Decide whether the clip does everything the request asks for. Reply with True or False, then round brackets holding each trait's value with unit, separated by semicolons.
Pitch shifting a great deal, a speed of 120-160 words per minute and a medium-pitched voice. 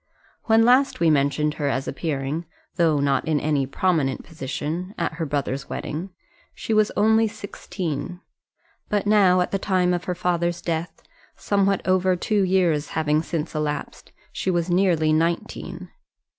False (3.8 semitones; 150 wpm; 170 Hz)